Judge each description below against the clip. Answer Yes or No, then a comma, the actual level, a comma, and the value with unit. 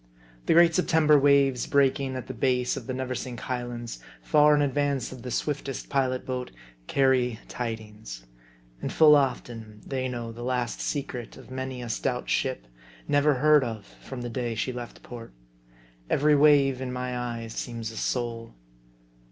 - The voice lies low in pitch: Yes, low, 130 Hz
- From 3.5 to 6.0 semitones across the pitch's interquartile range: No, narrow, 2.5 semitones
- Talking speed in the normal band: Yes, average, 160 wpm